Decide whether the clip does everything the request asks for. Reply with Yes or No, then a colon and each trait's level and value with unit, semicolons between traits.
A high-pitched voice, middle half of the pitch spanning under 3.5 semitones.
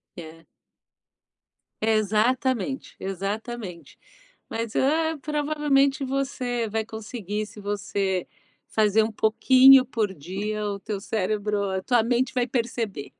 No: high, 220 Hz; average, 4.1 semitones